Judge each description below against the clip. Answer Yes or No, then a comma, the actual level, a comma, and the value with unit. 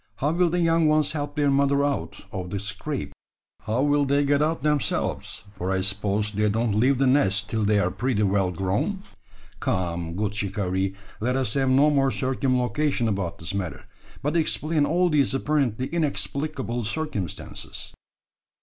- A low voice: Yes, low, 130 Hz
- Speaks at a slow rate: No, average, 165 wpm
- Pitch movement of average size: No, wide, 6.3 semitones